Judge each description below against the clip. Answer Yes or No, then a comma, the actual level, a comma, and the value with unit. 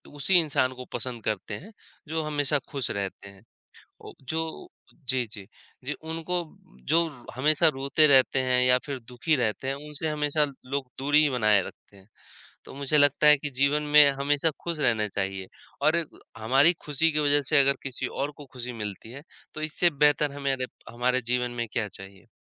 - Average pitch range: Yes, average, 3.5 semitones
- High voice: No, medium, 140 Hz